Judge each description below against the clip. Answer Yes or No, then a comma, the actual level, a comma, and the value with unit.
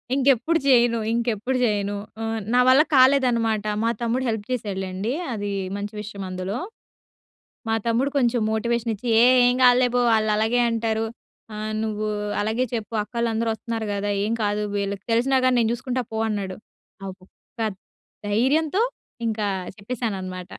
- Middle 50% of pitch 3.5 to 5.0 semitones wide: No, average, 3.0 semitones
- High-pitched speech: Yes, high, 225 Hz